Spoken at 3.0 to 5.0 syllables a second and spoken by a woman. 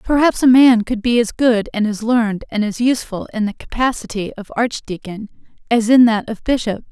No: 5.3 syllables/s; female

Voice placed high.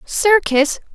Yes: very high, 340 Hz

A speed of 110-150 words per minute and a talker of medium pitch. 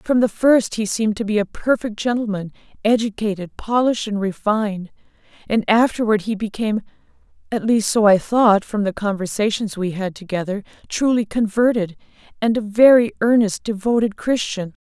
No: average, 140 wpm; high, 215 Hz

